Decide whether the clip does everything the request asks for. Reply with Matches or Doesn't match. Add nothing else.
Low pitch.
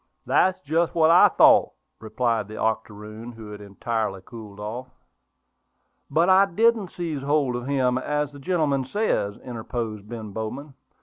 Matches